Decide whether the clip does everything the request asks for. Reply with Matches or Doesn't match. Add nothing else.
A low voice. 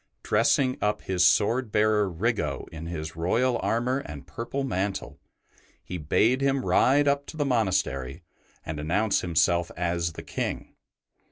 Matches